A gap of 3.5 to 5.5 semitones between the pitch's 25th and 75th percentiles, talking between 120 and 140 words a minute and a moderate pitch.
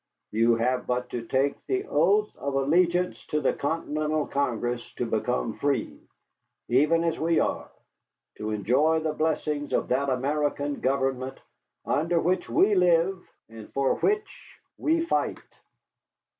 Yes: average, 4.5 semitones; slow, 135 wpm; medium, 145 Hz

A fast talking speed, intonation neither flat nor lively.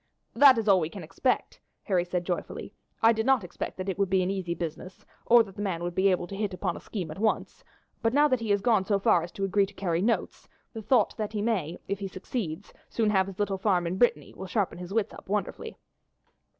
Yes: fast, 250 wpm; average, 3.3 semitones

